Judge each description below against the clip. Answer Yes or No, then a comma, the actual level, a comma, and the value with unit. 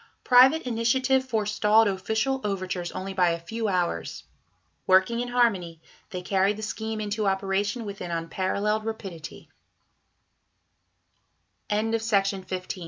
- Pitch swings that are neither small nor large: Yes, average, 3.3 semitones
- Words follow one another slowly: Yes, slow, 105 wpm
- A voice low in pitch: No, high, 210 Hz